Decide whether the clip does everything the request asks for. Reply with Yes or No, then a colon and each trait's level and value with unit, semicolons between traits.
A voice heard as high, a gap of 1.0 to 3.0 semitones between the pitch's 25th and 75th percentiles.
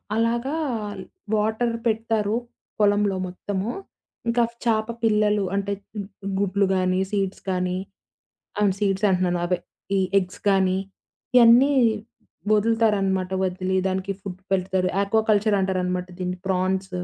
Yes: high, 195 Hz; narrow, 2.6 semitones